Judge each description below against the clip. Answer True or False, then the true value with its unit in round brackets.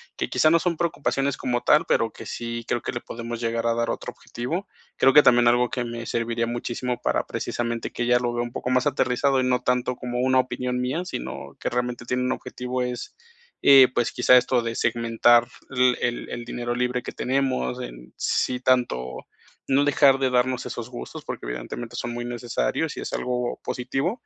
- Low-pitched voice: True (125 Hz)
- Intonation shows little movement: True (1.3 semitones)